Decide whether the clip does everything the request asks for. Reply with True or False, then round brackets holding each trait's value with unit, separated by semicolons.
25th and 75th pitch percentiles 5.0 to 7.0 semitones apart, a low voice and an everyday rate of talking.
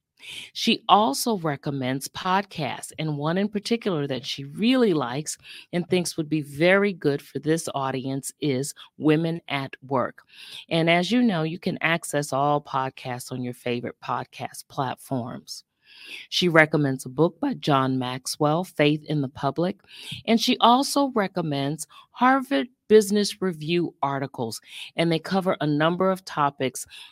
False (5.3 semitones; 160 Hz; 145 wpm)